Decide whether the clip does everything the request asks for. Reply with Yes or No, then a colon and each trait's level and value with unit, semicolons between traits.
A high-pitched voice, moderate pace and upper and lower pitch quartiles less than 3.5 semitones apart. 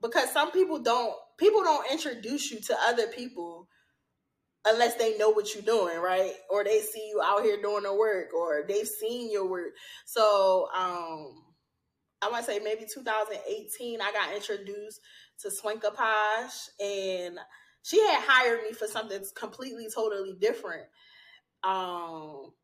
Yes: high, 215 Hz; average, 150 wpm; average, 2.8 semitones